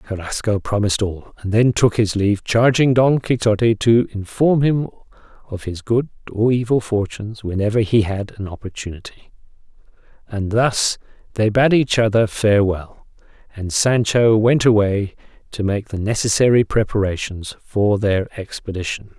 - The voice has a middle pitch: No, low, 110 Hz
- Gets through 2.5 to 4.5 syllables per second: No, 4.8 syllables/s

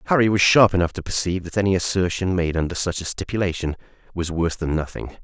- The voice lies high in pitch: No, very low, 90 Hz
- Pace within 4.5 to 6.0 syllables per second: No, 6.7 syllables/s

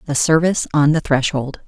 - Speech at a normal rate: Yes, average, 180 wpm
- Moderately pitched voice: Yes, medium, 150 Hz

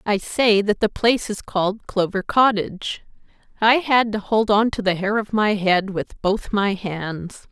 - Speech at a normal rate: Yes, average, 190 wpm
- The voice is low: No, high, 205 Hz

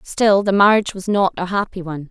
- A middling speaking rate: No, fast, 230 wpm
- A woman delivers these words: Yes, female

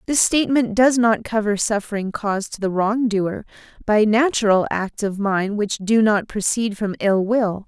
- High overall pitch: Yes, high, 215 Hz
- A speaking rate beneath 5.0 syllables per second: Yes, 4.6 syllables/s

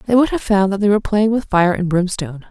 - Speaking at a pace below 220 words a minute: No, fast, 285 wpm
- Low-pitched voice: No, high, 200 Hz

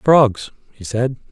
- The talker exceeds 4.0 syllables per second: No, 3.2 syllables/s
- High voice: No, low, 125 Hz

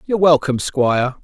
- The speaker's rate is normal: Yes, average, 145 wpm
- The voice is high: No, medium, 145 Hz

